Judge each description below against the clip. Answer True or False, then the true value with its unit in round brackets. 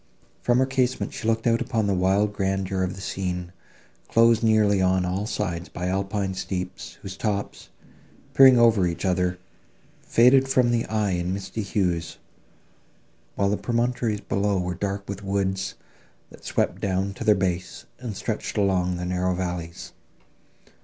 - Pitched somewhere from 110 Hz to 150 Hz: False (100 Hz)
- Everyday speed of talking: True (155 wpm)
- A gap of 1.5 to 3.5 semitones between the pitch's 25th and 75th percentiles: True (3.1 semitones)